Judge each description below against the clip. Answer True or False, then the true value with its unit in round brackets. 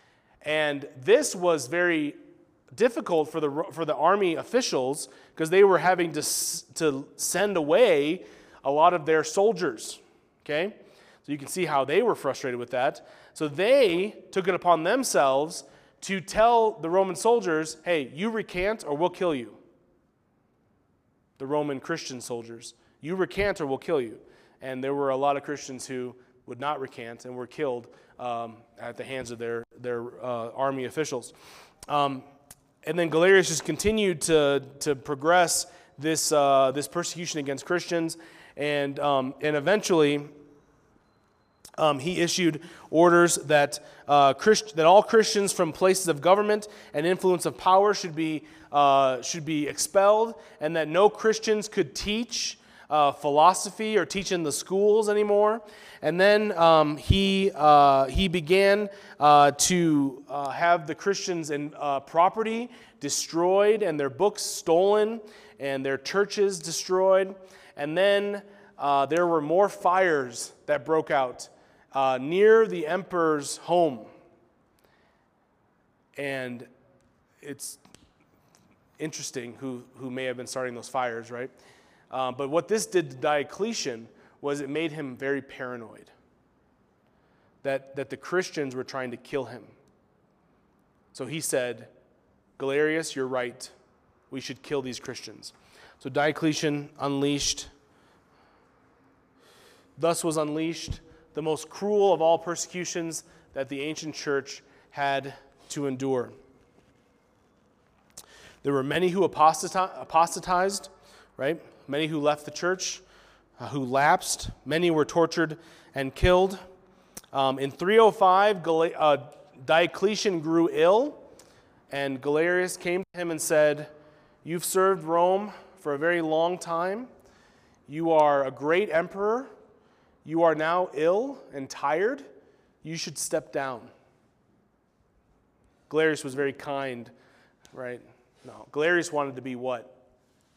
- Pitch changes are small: False (5.1 semitones)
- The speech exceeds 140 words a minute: False (135 wpm)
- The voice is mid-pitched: True (155 Hz)